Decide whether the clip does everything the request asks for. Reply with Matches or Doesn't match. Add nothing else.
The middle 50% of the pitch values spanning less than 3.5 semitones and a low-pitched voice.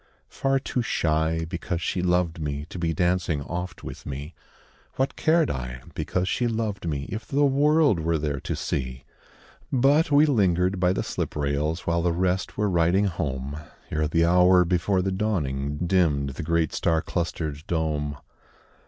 Doesn't match